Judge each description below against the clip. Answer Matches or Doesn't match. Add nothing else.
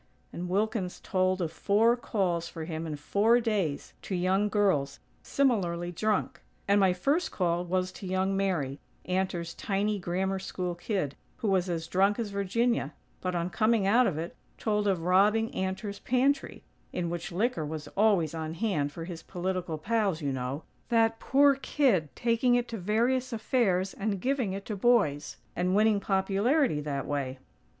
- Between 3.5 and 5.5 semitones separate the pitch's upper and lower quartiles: Matches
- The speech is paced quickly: Doesn't match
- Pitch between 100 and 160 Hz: Doesn't match